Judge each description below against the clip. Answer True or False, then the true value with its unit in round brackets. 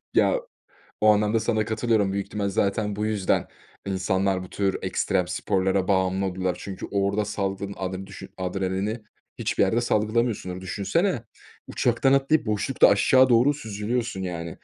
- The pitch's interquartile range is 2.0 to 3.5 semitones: True (2.7 semitones)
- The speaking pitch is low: True (100 Hz)